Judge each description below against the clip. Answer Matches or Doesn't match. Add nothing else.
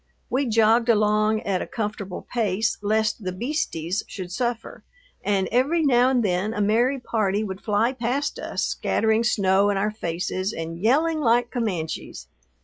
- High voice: Matches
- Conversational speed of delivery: Matches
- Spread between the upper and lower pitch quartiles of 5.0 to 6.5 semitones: Doesn't match